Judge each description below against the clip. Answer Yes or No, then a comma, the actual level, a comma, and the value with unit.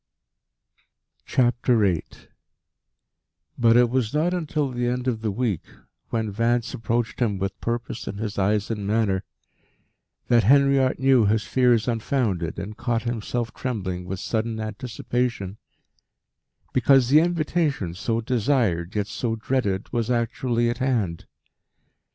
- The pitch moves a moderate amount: Yes, average, 3.3 semitones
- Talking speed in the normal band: No, slow, 125 wpm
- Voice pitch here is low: Yes, low, 115 Hz